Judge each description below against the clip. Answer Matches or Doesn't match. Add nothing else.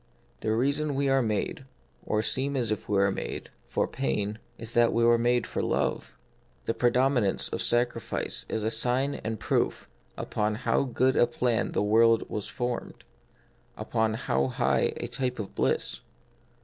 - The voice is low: Matches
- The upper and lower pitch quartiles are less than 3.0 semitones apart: Matches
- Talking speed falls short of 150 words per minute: Doesn't match